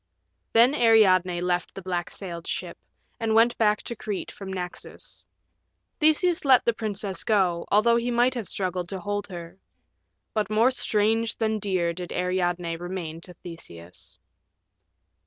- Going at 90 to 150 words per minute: Yes, average, 145 wpm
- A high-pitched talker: Yes, high, 195 Hz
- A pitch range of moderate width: Yes, average, 4.2 semitones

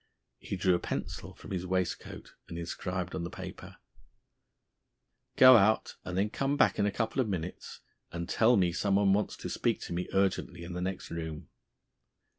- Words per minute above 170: Yes, average, 180 wpm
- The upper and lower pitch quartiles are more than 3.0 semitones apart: No, average, 2.7 semitones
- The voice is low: Yes, very low, 95 Hz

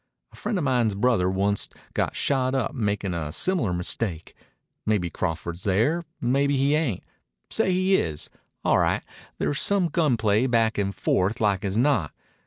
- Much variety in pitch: Yes, wide, 6.6 semitones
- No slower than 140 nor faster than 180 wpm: Yes, average, 165 wpm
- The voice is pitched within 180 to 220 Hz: No, low, 110 Hz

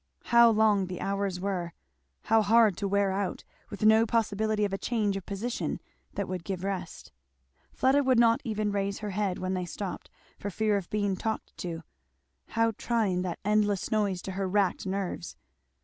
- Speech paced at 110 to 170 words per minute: No, average, 180 wpm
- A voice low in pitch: No, high, 200 Hz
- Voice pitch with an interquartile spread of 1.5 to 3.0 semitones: Yes, narrow, 2.4 semitones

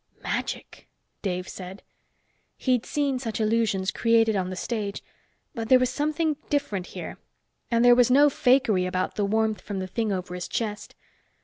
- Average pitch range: Yes, average, 4.7 semitones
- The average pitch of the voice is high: Yes, high, 220 Hz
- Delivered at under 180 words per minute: Yes, average, 165 wpm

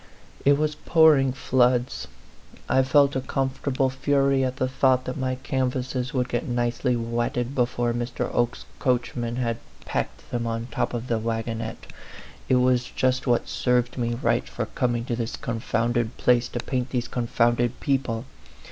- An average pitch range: No, narrow, 1.7 semitones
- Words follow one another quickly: No, average, 175 wpm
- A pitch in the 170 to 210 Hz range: No, low, 125 Hz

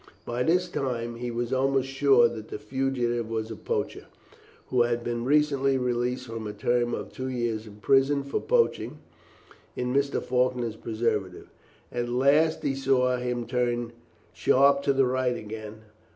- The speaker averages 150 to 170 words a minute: Yes, average, 160 wpm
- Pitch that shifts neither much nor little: No, narrow, 2.3 semitones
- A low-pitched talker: Yes, low, 125 Hz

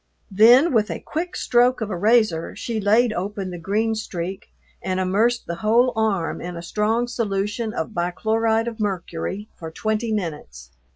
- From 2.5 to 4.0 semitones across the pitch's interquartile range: Yes, average, 3.7 semitones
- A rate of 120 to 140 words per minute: No, average, 165 wpm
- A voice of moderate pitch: No, high, 215 Hz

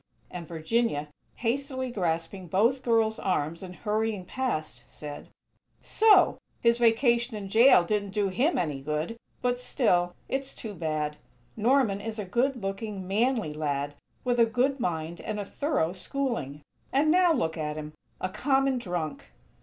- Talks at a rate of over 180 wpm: No, average, 150 wpm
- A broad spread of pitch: Yes, wide, 6.9 semitones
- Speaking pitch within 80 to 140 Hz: No, high, 210 Hz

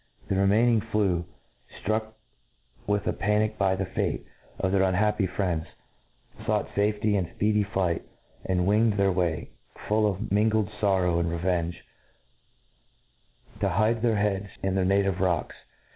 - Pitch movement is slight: Yes, narrow, 2.3 semitones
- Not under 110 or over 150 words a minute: Yes, average, 140 wpm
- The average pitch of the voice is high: No, low, 100 Hz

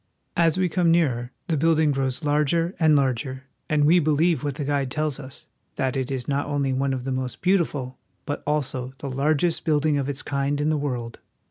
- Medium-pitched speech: Yes, medium, 145 Hz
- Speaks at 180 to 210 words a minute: Yes, fast, 205 wpm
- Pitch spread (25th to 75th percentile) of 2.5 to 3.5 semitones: Yes, average, 2.8 semitones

